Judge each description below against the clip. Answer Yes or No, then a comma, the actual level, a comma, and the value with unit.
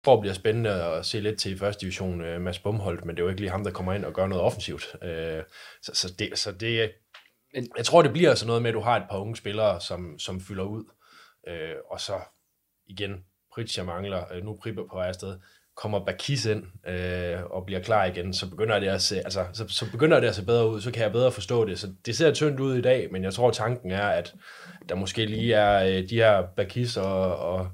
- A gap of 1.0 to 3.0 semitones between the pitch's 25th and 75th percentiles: No, average, 3.6 semitones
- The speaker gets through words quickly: Yes, fast, 255 wpm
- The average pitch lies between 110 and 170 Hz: No, low, 100 Hz